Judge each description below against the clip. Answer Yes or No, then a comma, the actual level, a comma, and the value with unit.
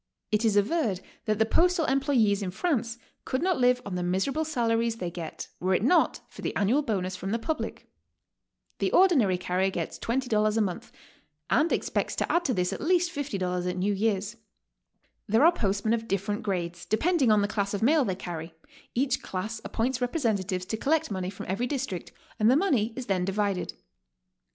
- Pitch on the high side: Yes, high, 220 Hz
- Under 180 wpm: No, average, 190 wpm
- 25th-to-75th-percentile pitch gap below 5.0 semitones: No, wide, 5.5 semitones